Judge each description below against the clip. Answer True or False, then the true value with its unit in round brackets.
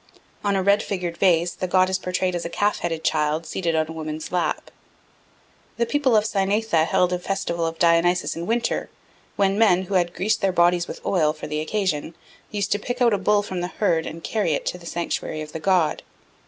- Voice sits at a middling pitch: True (180 Hz)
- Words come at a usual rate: False (220 wpm)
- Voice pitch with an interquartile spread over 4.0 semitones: False (3.3 semitones)